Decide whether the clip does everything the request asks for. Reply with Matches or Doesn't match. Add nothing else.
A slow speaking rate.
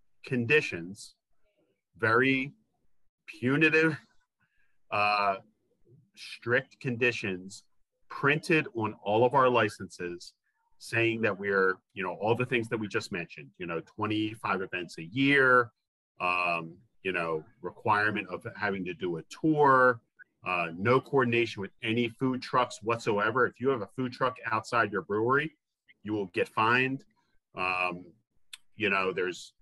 Matches